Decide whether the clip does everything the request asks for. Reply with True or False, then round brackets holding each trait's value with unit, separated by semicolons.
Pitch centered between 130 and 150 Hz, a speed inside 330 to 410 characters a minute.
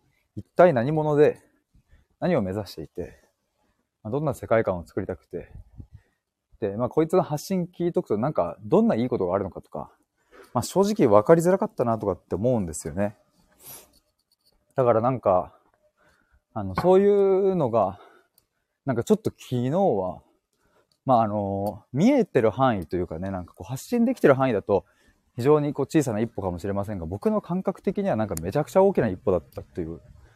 True (135 Hz; 360 characters per minute)